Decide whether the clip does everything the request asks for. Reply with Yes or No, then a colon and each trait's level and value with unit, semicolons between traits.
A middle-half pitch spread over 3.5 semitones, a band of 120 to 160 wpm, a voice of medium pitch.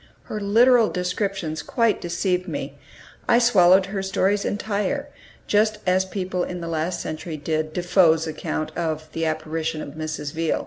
Yes: average, 4.1 semitones; average, 150 wpm; medium, 180 Hz